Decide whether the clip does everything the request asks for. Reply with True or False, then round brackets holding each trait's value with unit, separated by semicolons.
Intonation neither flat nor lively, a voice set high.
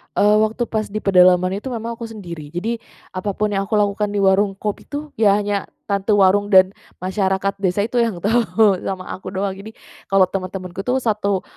False (2.1 semitones; 200 Hz)